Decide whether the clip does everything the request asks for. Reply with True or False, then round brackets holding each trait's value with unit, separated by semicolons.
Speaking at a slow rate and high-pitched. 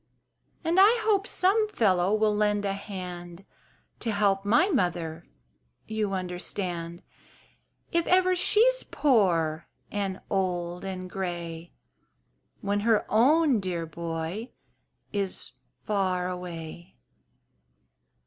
True (100 wpm; 195 Hz)